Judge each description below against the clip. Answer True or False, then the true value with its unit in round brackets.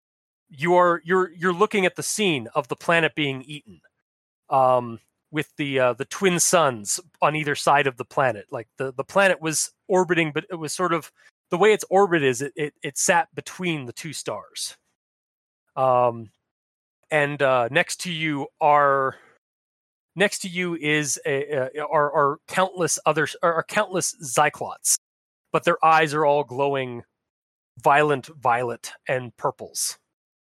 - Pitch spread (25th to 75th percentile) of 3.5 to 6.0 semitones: True (4.1 semitones)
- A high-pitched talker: False (150 Hz)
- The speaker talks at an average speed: True (160 wpm)